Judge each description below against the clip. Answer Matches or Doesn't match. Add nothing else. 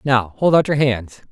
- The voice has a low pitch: Matches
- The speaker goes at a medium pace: Doesn't match